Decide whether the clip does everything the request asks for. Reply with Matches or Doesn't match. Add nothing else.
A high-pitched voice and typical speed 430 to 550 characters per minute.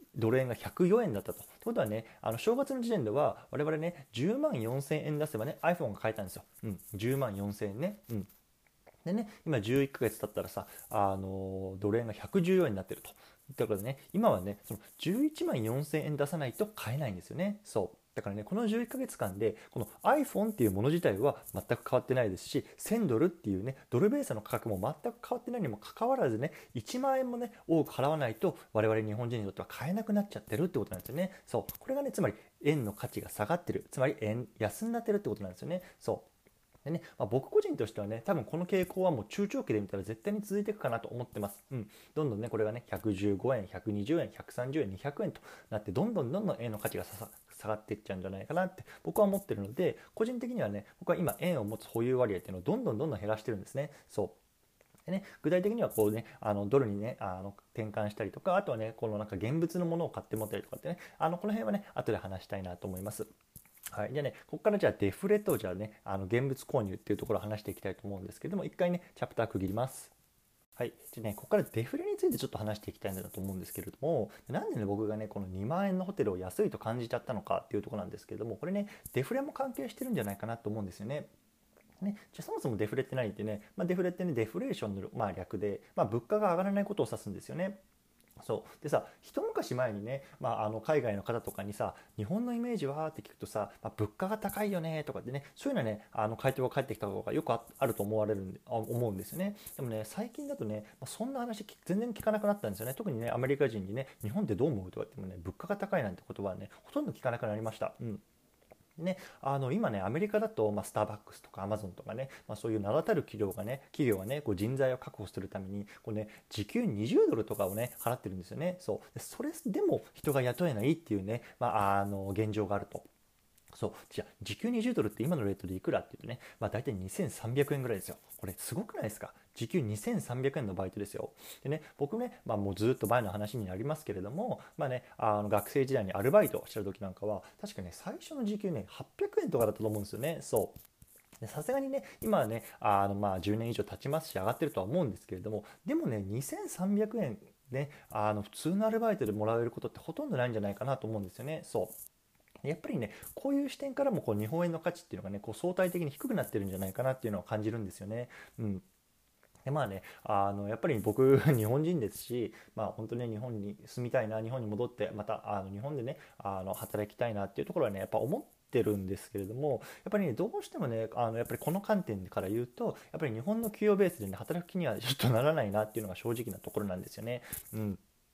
Doesn't match